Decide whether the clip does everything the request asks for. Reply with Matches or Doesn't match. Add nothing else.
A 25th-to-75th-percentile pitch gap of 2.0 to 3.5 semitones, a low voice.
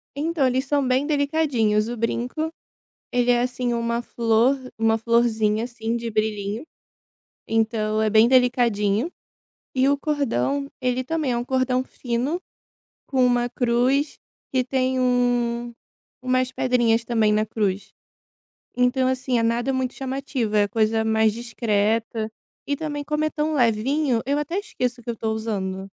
Doesn't match